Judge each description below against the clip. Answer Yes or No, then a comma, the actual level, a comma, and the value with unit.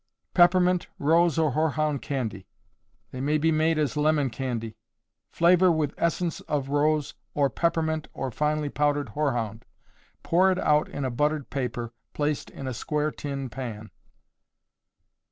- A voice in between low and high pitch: Yes, medium, 150 Hz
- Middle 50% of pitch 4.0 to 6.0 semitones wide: No, average, 3.1 semitones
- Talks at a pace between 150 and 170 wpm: No, average, 140 wpm